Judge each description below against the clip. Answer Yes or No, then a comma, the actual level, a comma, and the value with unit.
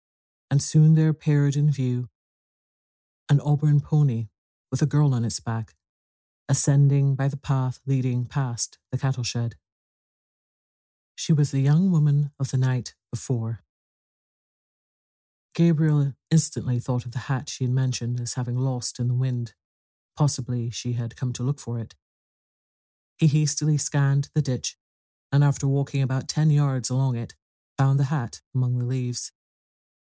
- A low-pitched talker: Yes, low, 130 Hz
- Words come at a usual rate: Yes, average, 150 wpm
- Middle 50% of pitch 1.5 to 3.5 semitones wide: Yes, average, 3.0 semitones